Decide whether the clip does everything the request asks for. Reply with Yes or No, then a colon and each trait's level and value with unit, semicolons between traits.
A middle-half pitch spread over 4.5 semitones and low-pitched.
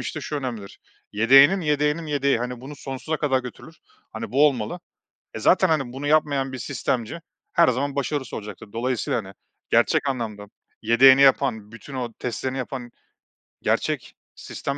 No: average, 3.4 semitones; low, 130 Hz